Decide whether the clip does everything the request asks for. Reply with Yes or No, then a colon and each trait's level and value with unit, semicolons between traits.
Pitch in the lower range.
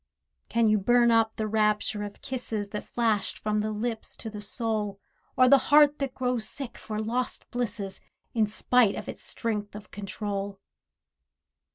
No: high, 220 Hz